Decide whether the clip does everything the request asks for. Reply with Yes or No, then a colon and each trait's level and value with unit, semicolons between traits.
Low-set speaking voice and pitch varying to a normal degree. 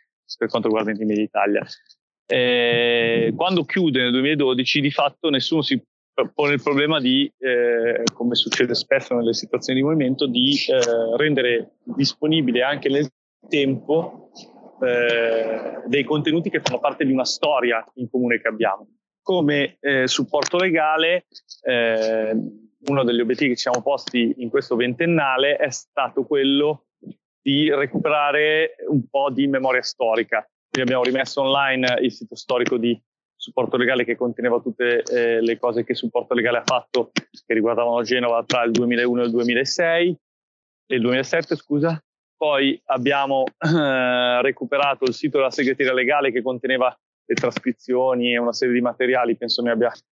Yes: low, 130 Hz; average, 3.4 semitones